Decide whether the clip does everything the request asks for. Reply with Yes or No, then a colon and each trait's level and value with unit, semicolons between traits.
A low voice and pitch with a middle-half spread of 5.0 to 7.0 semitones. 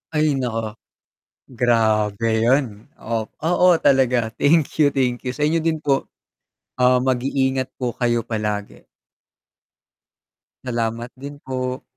No: low, 125 Hz; average, 3.0 semitones